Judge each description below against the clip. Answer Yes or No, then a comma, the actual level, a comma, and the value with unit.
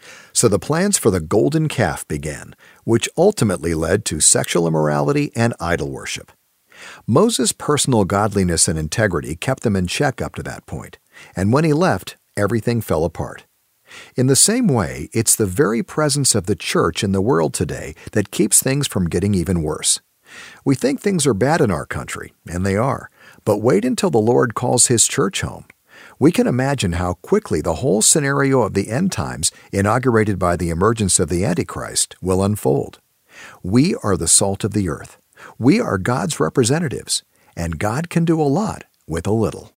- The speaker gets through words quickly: No, average, 180 wpm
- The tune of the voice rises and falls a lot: Yes, wide, 6.6 semitones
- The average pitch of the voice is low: Yes, low, 110 Hz